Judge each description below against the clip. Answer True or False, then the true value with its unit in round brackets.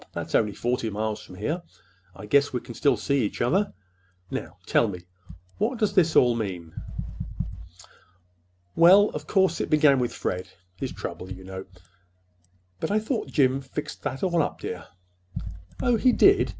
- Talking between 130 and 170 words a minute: True (160 wpm)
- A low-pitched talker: True (130 Hz)